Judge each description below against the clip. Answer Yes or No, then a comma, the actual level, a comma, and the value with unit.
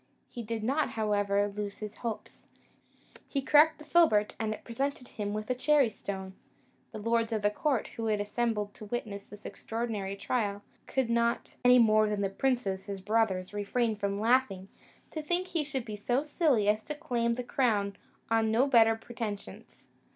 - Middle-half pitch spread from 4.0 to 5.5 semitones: No, average, 3.4 semitones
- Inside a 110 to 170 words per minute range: No, average, 180 wpm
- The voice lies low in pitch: No, high, 225 Hz